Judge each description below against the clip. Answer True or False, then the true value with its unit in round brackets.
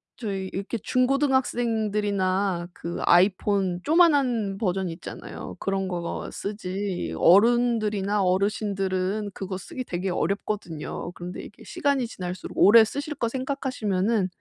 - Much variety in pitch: False (4.0 semitones)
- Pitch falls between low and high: False (200 Hz)